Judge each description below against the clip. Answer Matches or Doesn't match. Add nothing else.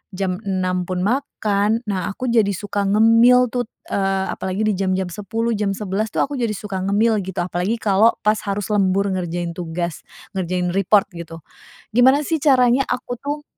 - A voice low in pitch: Doesn't match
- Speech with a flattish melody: Doesn't match